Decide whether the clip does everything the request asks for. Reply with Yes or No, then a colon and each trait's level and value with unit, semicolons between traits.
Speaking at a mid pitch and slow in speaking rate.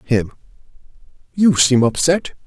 Yes: medium, 145 Hz; slow, 95 wpm